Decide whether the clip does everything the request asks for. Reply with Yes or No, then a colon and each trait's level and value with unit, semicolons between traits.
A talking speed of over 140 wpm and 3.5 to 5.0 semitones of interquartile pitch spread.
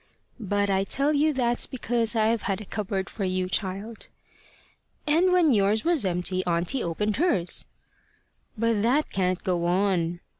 Yes: average, 150 wpm; average, 4.6 semitones